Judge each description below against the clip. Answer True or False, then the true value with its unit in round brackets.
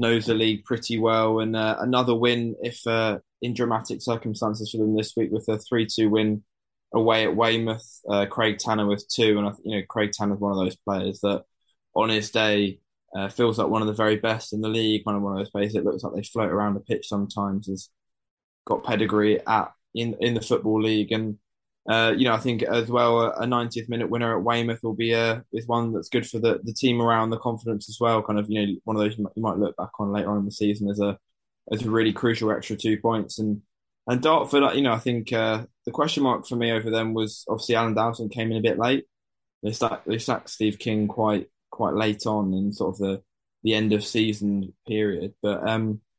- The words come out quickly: True (235 wpm)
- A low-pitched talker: True (110 Hz)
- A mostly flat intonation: True (1.7 semitones)